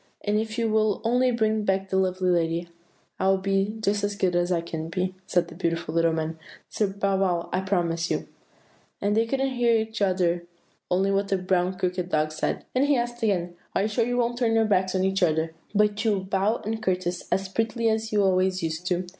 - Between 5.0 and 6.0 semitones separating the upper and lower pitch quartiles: No, average, 3.4 semitones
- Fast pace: Yes, fast, 225 wpm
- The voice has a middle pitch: No, high, 195 Hz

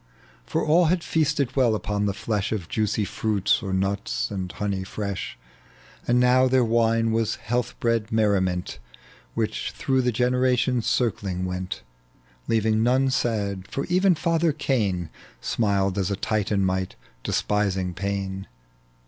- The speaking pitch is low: Yes, low, 110 Hz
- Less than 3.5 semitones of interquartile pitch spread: No, average, 4.3 semitones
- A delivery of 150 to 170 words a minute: No, average, 140 wpm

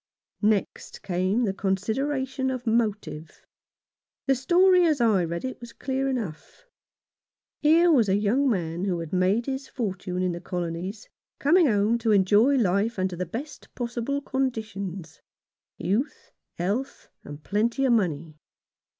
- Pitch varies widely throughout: Yes, wide, 6.1 semitones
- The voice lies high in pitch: Yes, high, 215 Hz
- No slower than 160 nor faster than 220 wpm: No, average, 140 wpm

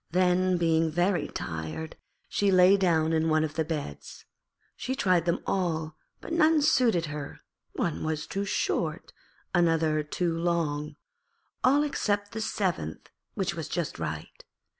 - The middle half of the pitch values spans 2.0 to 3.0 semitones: No, average, 3.5 semitones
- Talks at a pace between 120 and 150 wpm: Yes, average, 140 wpm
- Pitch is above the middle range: No, medium, 170 Hz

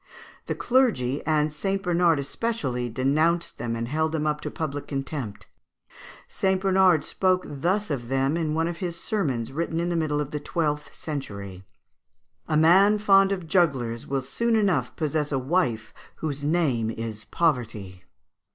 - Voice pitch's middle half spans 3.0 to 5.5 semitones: Yes, average, 5.0 semitones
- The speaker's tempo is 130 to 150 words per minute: No, average, 160 wpm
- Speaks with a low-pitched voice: No, medium, 155 Hz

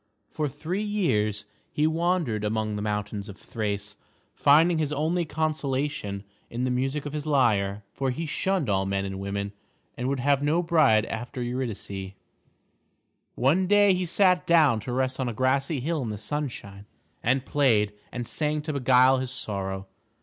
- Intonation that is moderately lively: No, wide, 6.3 semitones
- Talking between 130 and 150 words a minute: No, average, 165 wpm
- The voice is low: Yes, low, 130 Hz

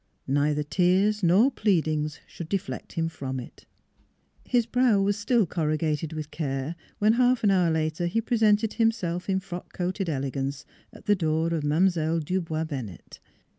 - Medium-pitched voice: Yes, medium, 170 Hz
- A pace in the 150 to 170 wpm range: Yes, average, 165 wpm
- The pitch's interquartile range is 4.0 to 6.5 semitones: Yes, average, 4.9 semitones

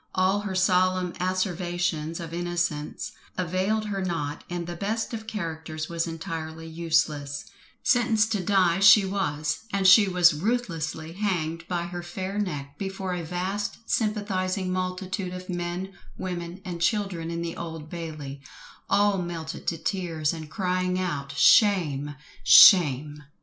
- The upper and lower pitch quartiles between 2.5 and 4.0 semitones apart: Yes, average, 2.8 semitones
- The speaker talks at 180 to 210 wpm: No, average, 140 wpm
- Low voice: No, medium, 175 Hz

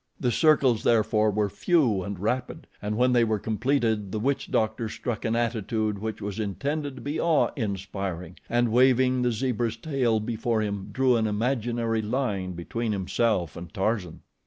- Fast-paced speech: No, average, 165 wpm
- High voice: No, low, 115 Hz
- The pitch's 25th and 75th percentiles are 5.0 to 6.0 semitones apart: No, average, 3.2 semitones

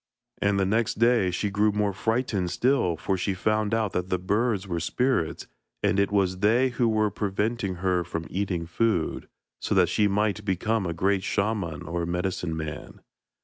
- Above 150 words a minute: Yes, average, 180 wpm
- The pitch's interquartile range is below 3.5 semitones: Yes, average, 3.1 semitones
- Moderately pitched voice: No, low, 100 Hz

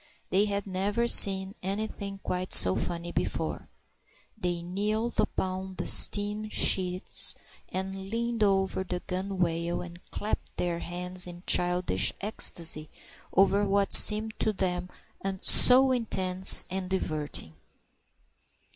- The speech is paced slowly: Yes, slow, 110 wpm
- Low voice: No, high, 190 Hz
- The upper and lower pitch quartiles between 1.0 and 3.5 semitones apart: Yes, narrow, 2.4 semitones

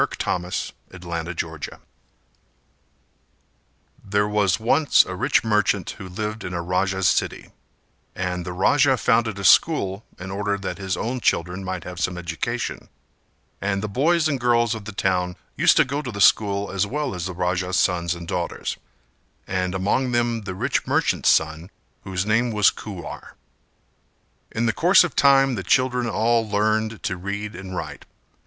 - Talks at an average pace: Yes, average, 170 wpm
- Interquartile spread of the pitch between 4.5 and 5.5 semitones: No, average, 4.0 semitones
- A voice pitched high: No, low, 100 Hz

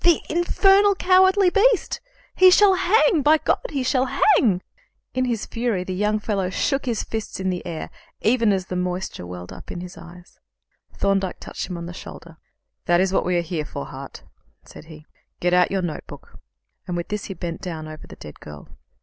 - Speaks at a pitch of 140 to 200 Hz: Yes, high, 190 Hz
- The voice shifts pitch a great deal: Yes, wide, 8.2 semitones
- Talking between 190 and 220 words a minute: Yes, average, 200 wpm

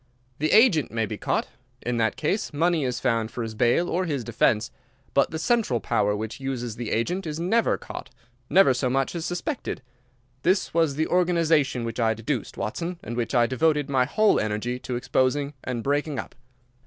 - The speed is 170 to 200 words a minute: Yes, average, 185 wpm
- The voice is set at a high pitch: No, low, 135 Hz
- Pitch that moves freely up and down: Yes, wide, 5.7 semitones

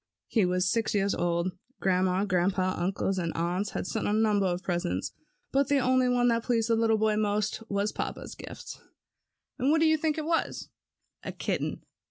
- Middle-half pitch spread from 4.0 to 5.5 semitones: Yes, average, 4.3 semitones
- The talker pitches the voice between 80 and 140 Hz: No, high, 205 Hz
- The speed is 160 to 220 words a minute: Yes, average, 185 wpm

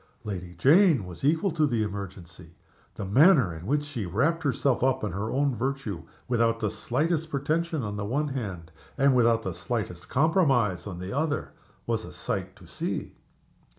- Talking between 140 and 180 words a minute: Yes, average, 175 wpm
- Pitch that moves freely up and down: Yes, wide, 6.7 semitones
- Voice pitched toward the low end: Yes, low, 120 Hz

